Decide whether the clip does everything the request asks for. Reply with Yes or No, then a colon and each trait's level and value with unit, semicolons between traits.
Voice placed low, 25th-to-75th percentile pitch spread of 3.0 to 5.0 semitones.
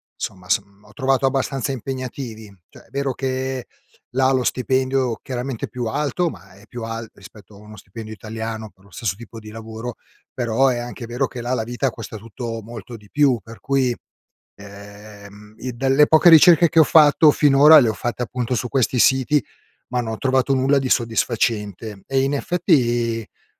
Yes: low, 120 Hz; average, 3.3 semitones